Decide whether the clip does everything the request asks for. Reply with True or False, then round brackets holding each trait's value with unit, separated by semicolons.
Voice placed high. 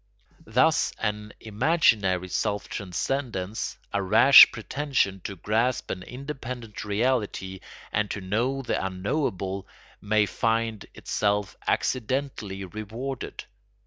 False (110 Hz)